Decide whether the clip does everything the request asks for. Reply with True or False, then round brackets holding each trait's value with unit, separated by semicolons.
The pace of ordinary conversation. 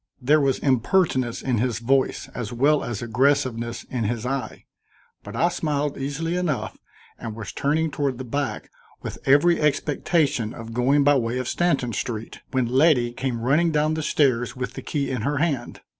True (175 wpm)